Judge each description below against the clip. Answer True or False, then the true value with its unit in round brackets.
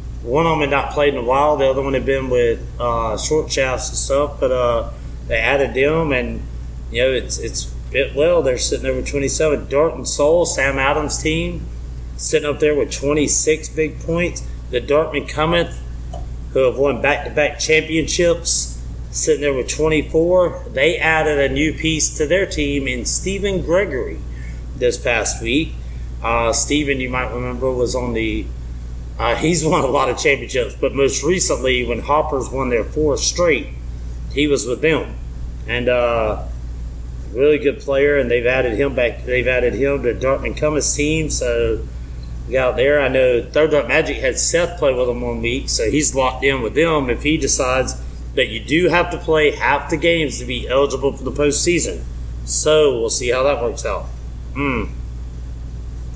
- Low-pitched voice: True (130 Hz)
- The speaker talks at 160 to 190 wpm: True (185 wpm)